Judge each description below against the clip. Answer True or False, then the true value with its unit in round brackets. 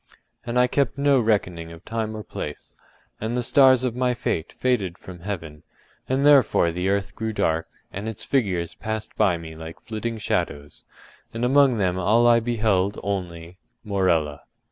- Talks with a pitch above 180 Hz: False (105 Hz)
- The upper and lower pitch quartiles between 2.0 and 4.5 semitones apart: False (5.4 semitones)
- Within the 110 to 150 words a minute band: False (165 wpm)